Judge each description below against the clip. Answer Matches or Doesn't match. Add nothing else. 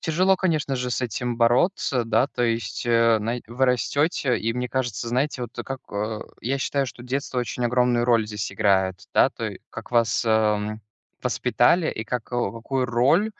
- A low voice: Matches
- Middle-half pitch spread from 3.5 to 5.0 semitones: Doesn't match